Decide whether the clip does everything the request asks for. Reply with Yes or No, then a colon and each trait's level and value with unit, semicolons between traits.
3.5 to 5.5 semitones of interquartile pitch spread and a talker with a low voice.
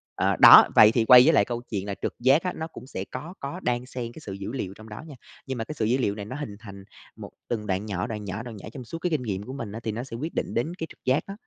Yes: average, 4.5 semitones; low, 120 Hz